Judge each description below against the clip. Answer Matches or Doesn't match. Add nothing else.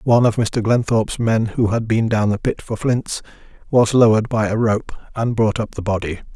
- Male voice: Matches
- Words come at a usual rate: Doesn't match